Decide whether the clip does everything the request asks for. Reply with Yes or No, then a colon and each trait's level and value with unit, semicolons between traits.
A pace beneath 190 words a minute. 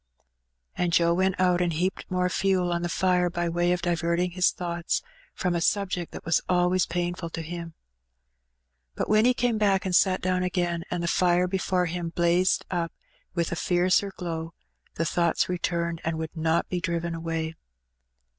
Yes: average, 180 wpm